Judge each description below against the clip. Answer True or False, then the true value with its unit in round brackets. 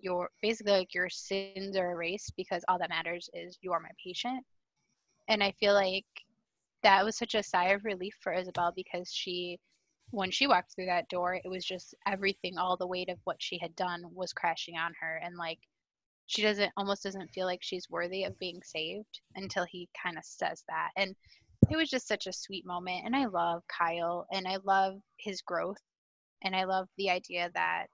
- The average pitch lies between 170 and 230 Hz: True (185 Hz)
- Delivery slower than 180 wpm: False (200 wpm)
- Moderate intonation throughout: False (1.9 semitones)